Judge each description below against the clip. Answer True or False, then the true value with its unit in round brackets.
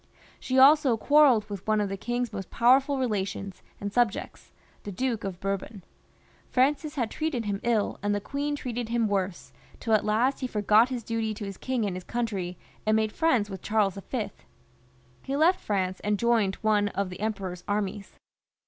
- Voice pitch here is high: True (215 Hz)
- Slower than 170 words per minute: False (185 wpm)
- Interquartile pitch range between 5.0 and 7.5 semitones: False (3.8 semitones)